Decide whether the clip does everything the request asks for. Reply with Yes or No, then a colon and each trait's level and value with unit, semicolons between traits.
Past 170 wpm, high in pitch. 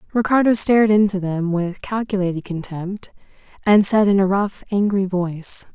No: average, 145 wpm; high, 195 Hz